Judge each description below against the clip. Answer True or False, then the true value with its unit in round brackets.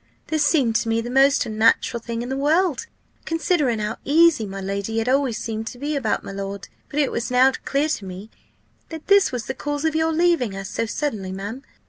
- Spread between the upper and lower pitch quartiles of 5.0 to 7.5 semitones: True (5.3 semitones)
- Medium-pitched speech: False (250 Hz)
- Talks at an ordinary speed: False (215 wpm)